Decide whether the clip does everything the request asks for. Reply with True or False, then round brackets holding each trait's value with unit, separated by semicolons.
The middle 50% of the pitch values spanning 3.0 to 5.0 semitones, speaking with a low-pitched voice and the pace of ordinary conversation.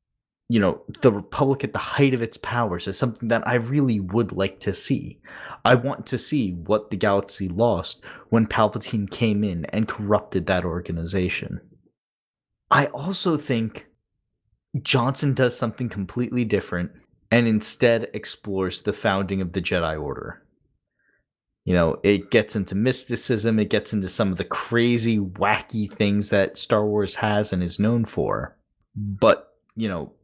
True (3.4 semitones; 105 Hz; 155 wpm)